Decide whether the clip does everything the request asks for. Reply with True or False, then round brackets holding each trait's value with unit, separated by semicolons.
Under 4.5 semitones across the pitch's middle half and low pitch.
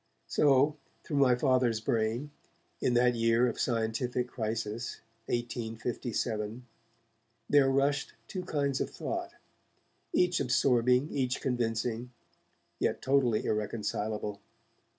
True (2.9 semitones; 120 Hz)